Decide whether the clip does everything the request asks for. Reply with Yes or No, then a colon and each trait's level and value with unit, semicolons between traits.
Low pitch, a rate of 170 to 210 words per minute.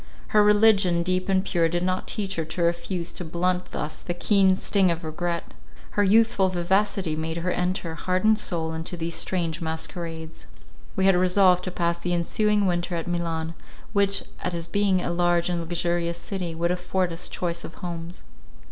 No: medium, 175 Hz; average, 180 wpm